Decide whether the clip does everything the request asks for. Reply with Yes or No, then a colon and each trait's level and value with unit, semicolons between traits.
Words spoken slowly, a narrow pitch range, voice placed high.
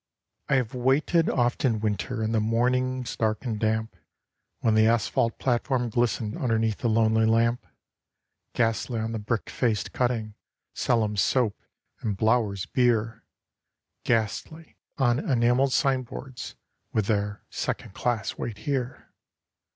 No: slow, 130 wpm; narrow, 2.3 semitones; low, 115 Hz